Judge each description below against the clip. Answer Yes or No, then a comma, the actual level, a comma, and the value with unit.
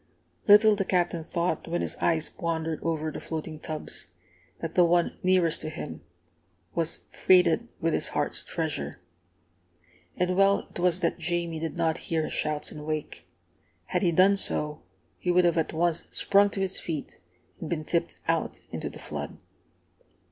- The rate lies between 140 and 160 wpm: No, average, 170 wpm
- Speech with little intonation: Yes, narrow, 2.2 semitones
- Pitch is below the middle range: No, medium, 170 Hz